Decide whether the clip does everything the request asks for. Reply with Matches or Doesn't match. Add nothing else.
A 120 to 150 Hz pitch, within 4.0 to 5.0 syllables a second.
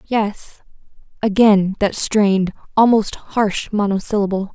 Doesn't match